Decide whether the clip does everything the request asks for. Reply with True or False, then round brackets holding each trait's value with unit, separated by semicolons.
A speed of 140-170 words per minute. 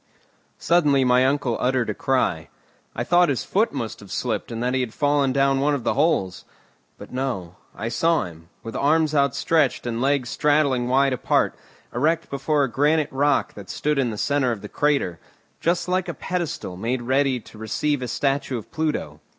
False (190 wpm)